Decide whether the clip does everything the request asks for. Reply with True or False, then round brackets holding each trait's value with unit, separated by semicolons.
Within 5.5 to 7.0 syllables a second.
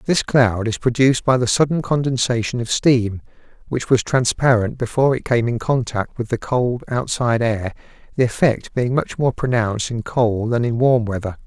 False (5.0 syllables/s)